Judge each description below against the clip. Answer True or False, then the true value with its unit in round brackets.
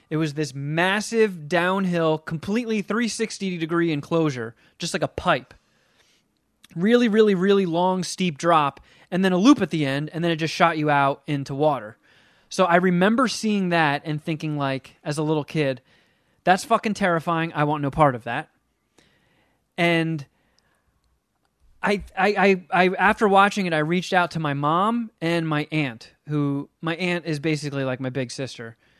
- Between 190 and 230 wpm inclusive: False (170 wpm)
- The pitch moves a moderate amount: True (4.2 semitones)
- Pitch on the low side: False (165 Hz)